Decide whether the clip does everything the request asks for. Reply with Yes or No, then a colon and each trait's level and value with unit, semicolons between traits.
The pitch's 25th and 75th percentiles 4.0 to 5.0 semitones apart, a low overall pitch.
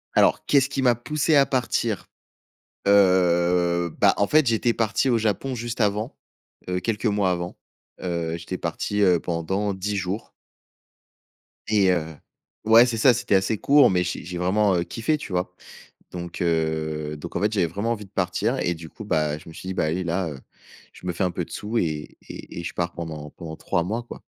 Yes: average, 4.5 semitones; very low, 95 Hz